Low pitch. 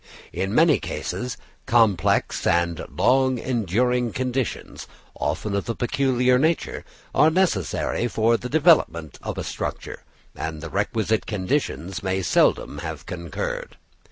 Yes: low, 115 Hz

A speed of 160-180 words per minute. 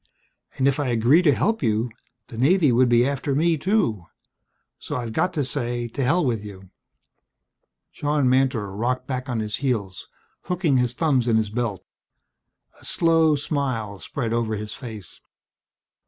Yes: average, 170 wpm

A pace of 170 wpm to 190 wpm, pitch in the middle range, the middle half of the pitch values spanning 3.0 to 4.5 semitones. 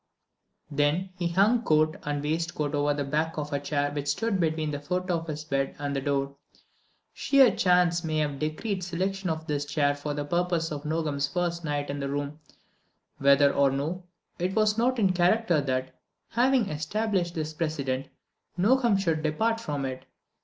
Yes: average, 175 wpm; medium, 155 Hz; average, 4.0 semitones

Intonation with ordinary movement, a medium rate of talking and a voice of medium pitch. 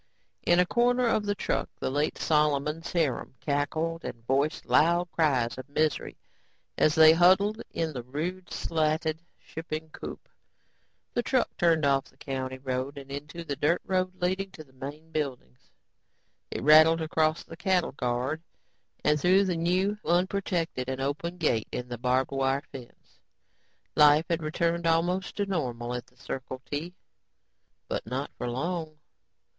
Yes: average, 4.2 semitones; average, 155 wpm; medium, 155 Hz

